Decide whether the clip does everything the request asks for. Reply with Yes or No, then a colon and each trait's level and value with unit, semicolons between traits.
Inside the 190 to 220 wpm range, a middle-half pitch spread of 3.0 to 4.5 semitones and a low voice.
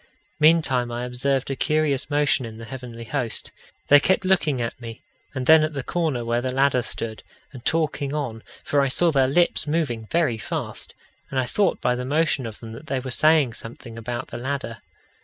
Yes: average, 200 wpm; average, 4.1 semitones; low, 130 Hz